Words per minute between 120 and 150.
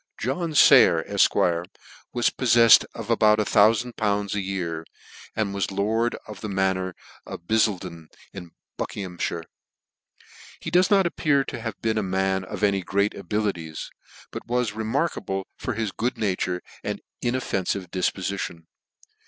Yes: average, 145 wpm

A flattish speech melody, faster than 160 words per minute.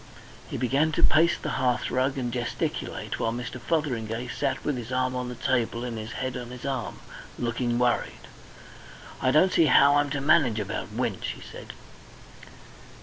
Yes: narrow, 2.3 semitones; average, 170 wpm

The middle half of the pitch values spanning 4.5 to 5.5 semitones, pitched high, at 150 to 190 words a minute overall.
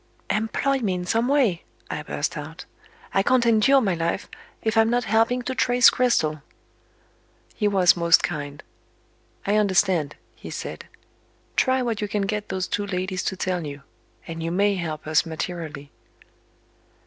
Yes: average, 5.1 semitones; high, 195 Hz; average, 160 wpm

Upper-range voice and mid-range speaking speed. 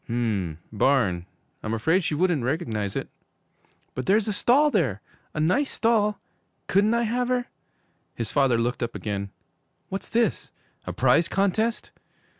No: medium, 160 Hz; average, 150 wpm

